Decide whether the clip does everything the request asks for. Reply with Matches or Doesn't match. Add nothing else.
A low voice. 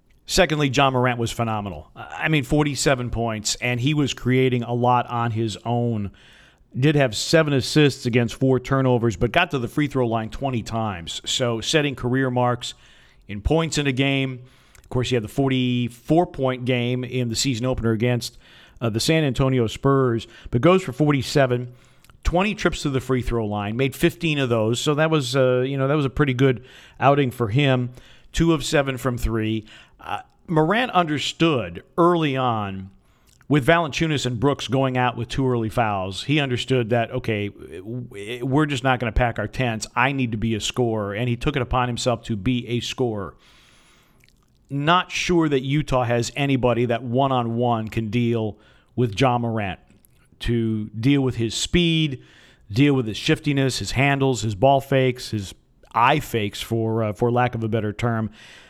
Matches